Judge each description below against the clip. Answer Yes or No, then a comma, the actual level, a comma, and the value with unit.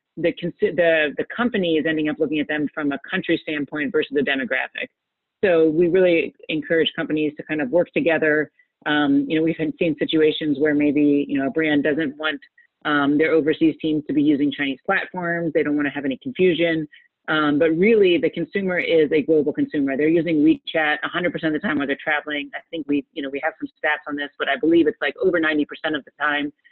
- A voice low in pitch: No, medium, 155 Hz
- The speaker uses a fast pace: Yes, fast, 225 wpm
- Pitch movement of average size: No, narrow, 2.3 semitones